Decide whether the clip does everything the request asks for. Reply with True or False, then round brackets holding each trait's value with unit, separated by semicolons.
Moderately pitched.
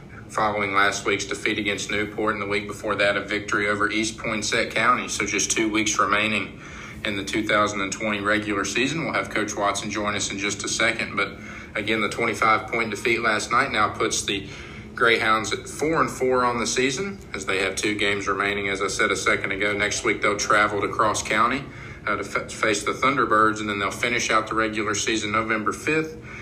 False (105 Hz)